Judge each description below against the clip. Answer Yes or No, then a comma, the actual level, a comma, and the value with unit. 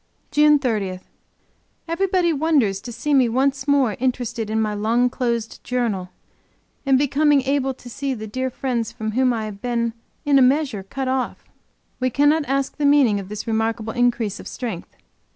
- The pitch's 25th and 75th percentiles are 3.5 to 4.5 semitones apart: Yes, average, 3.8 semitones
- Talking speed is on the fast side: No, average, 170 wpm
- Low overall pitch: No, very high, 250 Hz